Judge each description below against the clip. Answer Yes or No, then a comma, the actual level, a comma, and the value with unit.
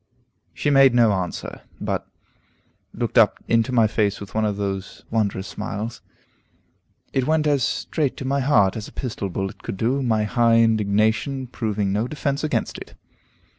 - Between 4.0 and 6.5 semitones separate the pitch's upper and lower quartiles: Yes, average, 4.3 semitones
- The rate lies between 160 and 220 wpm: Yes, average, 165 wpm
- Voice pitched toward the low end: Yes, low, 115 Hz